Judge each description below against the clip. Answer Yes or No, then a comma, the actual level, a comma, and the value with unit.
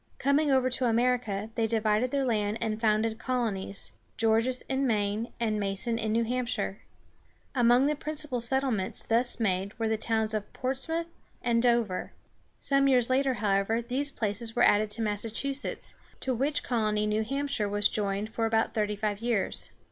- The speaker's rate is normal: Yes, average, 165 wpm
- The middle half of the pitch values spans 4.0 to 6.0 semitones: No, average, 3.1 semitones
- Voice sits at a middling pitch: No, high, 230 Hz